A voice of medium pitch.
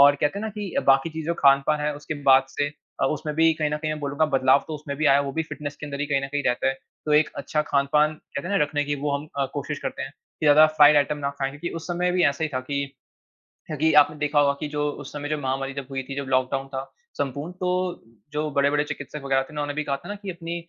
Yes: medium, 145 Hz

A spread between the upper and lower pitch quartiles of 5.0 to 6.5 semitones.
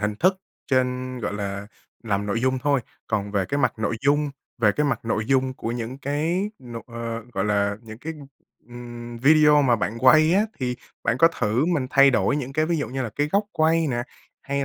No: average, 4.3 semitones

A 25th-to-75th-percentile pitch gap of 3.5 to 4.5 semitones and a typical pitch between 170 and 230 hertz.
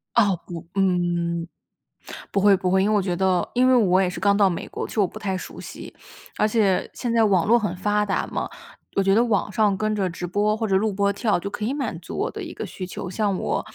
No: narrow, 2.5 semitones; high, 200 Hz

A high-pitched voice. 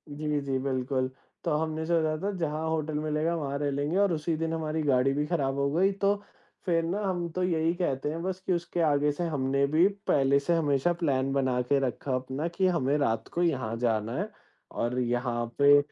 No: medium, 150 Hz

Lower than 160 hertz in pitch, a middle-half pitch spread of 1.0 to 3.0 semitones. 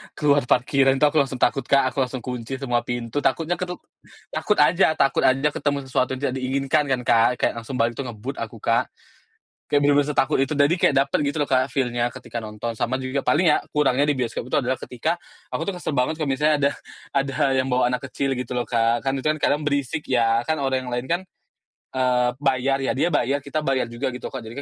Yes: low, 135 Hz; narrow, 2.5 semitones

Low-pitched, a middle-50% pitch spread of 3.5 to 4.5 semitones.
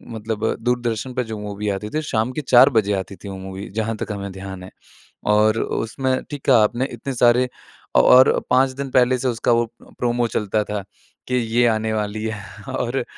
No: low, 110 Hz; average, 3.1 semitones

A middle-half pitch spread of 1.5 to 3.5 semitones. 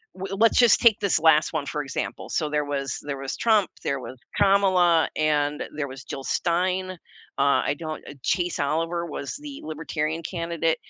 No: average, 4.1 semitones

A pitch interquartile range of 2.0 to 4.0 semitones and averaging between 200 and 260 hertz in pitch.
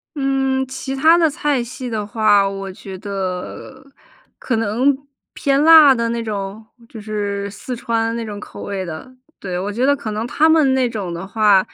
No: average, 4.8 semitones; high, 225 Hz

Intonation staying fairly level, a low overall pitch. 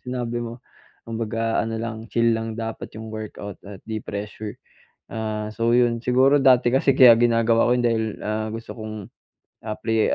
Yes: narrow, 1.6 semitones; low, 115 Hz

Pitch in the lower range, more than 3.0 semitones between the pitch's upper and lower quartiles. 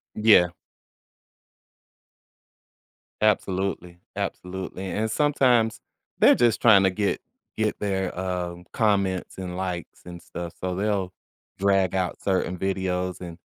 No: very low, 95 Hz; narrow, 2.4 semitones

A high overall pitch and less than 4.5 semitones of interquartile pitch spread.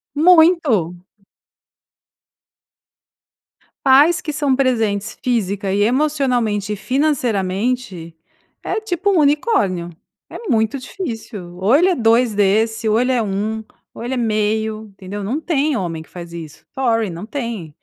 No: high, 225 Hz; wide, 5.4 semitones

